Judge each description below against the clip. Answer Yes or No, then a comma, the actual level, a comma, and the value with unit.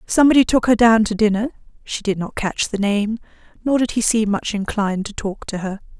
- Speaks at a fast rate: Yes, fast, 220 wpm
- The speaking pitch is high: Yes, high, 215 Hz